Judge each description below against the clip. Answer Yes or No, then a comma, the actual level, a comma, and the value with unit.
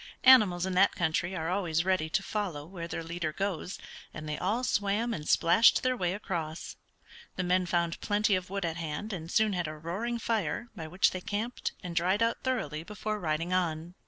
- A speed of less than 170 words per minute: No, average, 200 wpm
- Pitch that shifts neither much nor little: Yes, average, 3.8 semitones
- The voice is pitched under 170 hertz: No, medium, 180 Hz